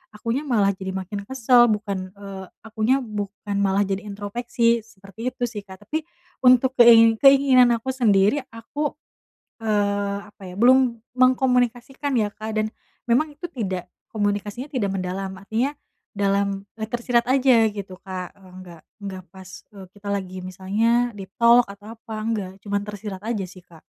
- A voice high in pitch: Yes, high, 215 Hz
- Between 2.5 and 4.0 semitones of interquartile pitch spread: Yes, average, 3.5 semitones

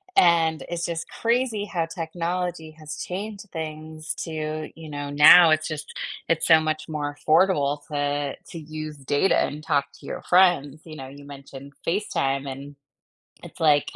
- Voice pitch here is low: No, medium, 155 Hz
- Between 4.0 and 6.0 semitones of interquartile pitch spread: No, narrow, 2.6 semitones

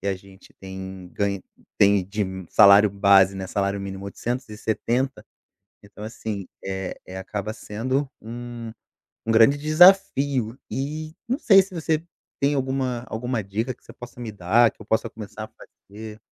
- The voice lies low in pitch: Yes, low, 110 Hz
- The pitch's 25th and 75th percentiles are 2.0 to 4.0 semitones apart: No, average, 4.7 semitones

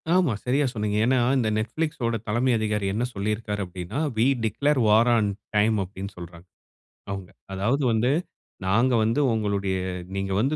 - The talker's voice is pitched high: No, low, 110 Hz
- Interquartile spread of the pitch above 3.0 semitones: Yes, average, 3.7 semitones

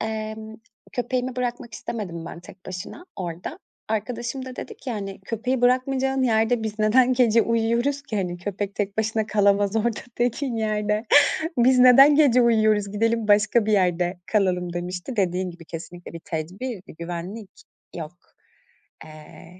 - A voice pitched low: No, high, 215 Hz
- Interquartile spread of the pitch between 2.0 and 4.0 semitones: No, average, 4.4 semitones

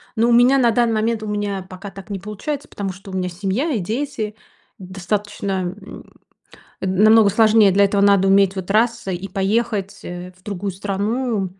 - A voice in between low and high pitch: No, high, 200 Hz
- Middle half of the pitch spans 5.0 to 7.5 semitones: No, narrow, 2.6 semitones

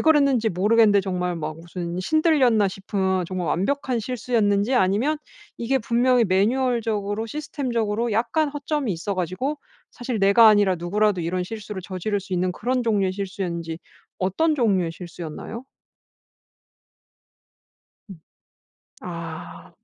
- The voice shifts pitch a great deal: No, average, 4.8 semitones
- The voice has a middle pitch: No, high, 205 Hz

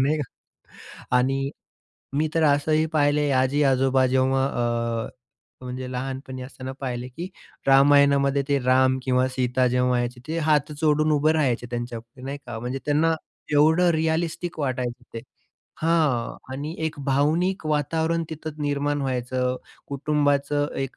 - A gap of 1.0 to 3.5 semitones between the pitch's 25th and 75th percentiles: Yes, average, 3.0 semitones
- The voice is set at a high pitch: No, medium, 140 Hz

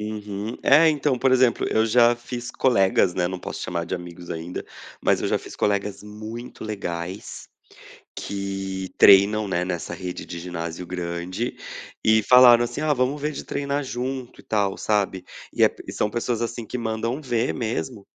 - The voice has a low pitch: Yes, low, 110 Hz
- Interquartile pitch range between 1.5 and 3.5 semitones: No, average, 4.7 semitones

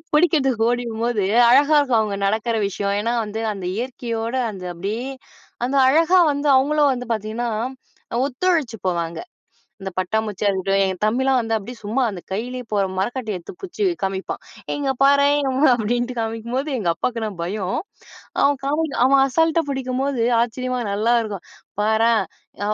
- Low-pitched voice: No, high, 235 Hz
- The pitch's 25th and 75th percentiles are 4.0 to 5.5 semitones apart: Yes, average, 4.3 semitones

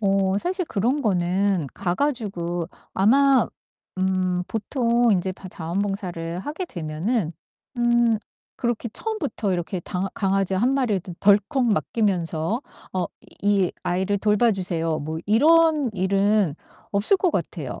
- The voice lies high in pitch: Yes, high, 200 Hz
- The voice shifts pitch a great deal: No, average, 4.8 semitones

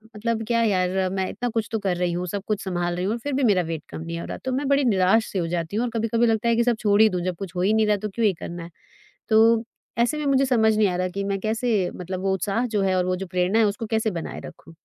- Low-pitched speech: No, high, 205 Hz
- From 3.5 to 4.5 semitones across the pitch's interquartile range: Yes, average, 3.8 semitones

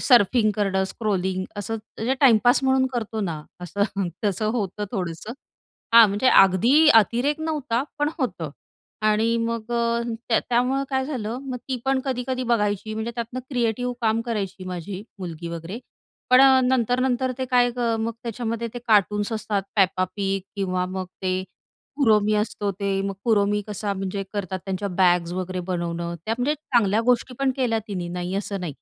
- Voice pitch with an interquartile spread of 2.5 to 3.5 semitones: No, average, 4.2 semitones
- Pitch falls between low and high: No, high, 215 Hz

